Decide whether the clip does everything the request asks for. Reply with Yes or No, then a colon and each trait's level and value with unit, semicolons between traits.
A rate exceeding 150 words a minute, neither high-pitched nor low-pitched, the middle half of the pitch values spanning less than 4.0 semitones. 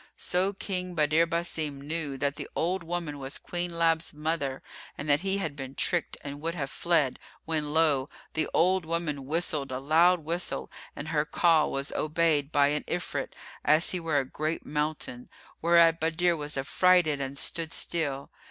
Yes: average, 170 wpm; medium, 155 Hz; average, 2.9 semitones